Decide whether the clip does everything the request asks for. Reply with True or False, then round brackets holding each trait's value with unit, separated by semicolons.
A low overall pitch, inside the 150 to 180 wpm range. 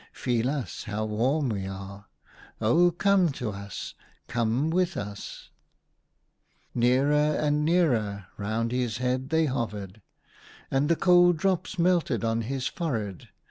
False (125 Hz; 135 wpm)